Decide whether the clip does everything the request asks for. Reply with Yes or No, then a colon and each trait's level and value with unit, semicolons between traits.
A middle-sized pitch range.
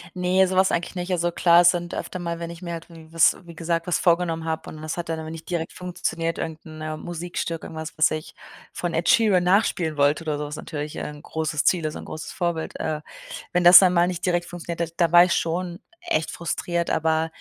No: narrow, 1.7 semitones